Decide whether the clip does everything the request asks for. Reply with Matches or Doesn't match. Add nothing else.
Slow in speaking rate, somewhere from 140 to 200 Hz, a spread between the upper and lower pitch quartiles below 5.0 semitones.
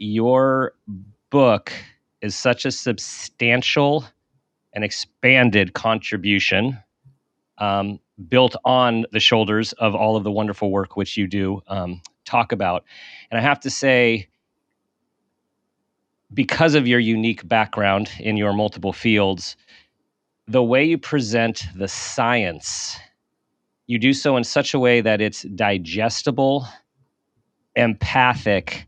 Doesn't match